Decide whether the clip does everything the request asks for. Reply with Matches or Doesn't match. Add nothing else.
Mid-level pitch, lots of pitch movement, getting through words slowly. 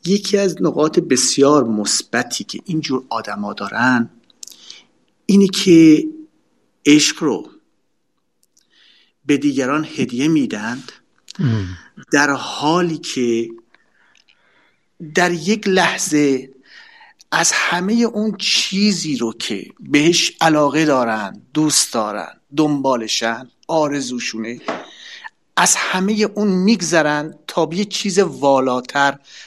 Matches